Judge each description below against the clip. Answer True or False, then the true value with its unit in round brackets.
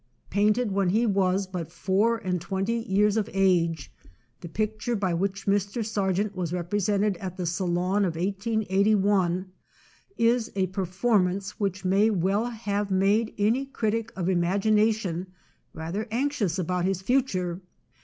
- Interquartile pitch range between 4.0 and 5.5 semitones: False (2.7 semitones)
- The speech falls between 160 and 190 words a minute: False (135 wpm)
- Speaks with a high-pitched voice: True (195 Hz)